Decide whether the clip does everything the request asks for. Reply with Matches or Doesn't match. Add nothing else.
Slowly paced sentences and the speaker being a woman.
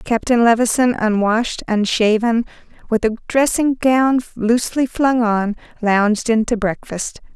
Matches